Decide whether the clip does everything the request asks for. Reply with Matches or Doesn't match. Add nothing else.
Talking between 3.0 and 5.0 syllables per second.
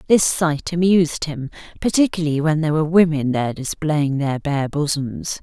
Doesn't match